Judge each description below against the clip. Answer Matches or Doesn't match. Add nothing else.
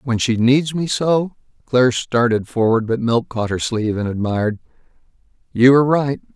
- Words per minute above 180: Doesn't match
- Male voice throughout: Matches